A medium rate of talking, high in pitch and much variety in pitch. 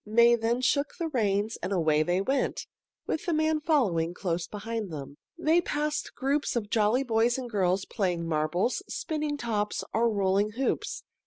Yes: average, 165 wpm; high, 225 Hz; wide, 6.3 semitones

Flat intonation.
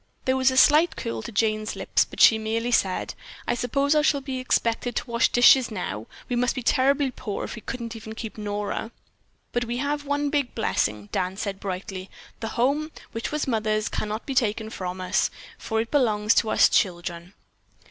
No: average, 3.9 semitones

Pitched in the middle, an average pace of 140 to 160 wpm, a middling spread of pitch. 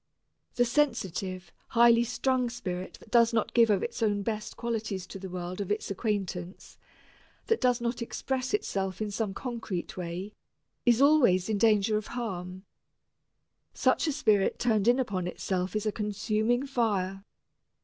No: high, 215 Hz; average, 155 wpm; average, 3.7 semitones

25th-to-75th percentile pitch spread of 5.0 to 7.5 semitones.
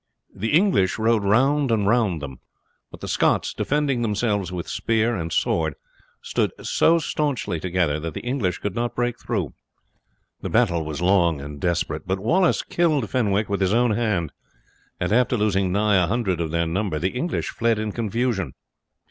Yes: average, 5.3 semitones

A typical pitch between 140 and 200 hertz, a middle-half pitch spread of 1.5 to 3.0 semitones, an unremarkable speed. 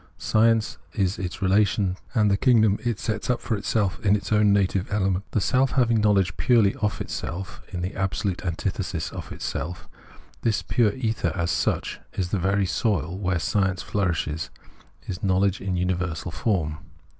No: low, 100 Hz; average, 2.7 semitones; average, 170 wpm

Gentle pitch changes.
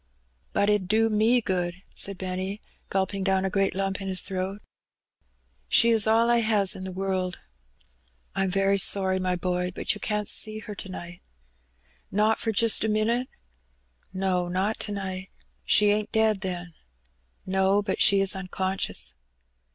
Yes: narrow, 2.1 semitones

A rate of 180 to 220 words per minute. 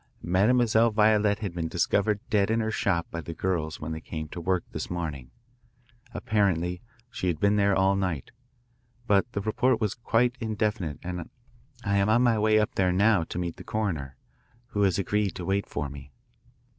Yes: average, 185 wpm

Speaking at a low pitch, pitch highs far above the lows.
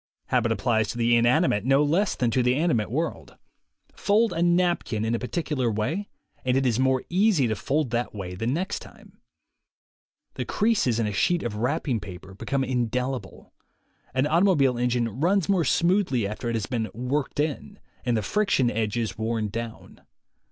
Yes: low, 125 Hz; wide, 5.8 semitones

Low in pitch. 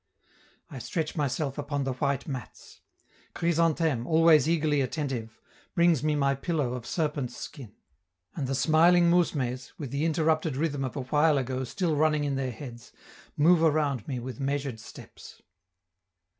No: medium, 145 Hz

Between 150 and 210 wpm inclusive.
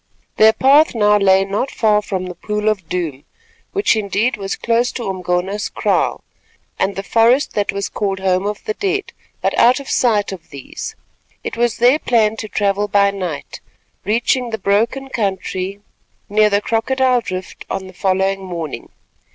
Yes: average, 165 wpm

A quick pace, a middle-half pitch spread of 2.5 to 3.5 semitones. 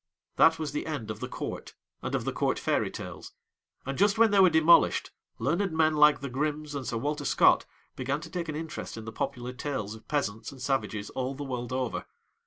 No: fast, 215 wpm; average, 4.0 semitones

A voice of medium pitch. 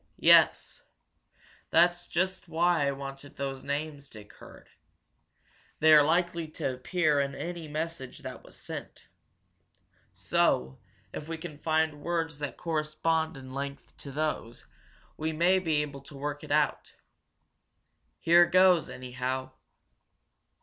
Yes: medium, 155 Hz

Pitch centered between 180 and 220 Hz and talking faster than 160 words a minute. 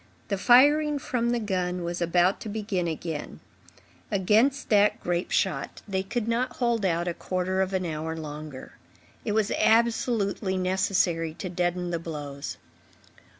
No: high, 190 Hz; average, 150 wpm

